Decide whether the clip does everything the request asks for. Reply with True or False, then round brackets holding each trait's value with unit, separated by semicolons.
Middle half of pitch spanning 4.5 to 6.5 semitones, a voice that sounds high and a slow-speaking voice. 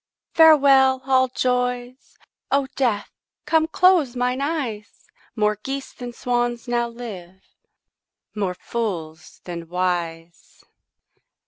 True (5.1 semitones; 245 Hz; 100 wpm)